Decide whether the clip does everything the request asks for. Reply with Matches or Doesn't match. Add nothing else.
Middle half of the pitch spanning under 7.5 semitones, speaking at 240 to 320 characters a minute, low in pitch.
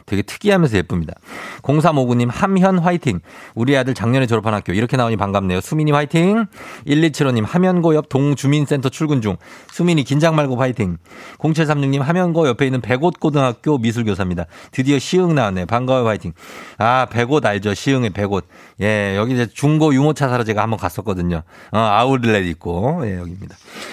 Doesn't match